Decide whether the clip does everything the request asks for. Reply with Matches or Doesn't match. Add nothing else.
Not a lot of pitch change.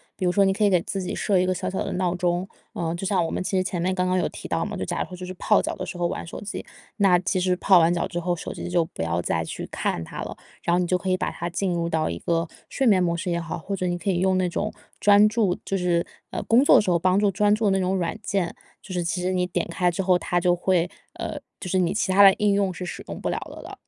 Matches